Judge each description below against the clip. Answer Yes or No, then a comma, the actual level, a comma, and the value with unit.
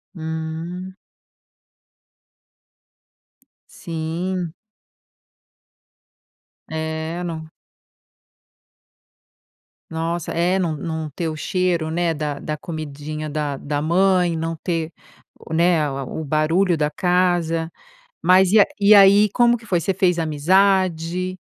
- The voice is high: No, medium, 165 Hz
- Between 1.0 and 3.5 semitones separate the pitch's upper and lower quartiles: Yes, narrow, 2.5 semitones